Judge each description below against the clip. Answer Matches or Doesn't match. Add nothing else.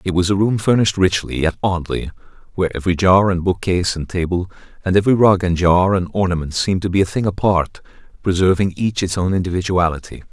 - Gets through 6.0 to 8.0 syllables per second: Matches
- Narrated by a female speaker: Doesn't match